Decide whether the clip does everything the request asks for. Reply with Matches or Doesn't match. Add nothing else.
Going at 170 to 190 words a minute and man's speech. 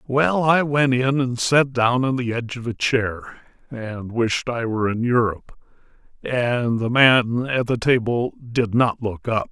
Matches